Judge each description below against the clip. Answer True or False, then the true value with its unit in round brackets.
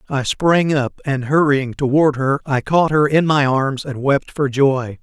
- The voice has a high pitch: False (140 Hz)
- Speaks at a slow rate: False (205 wpm)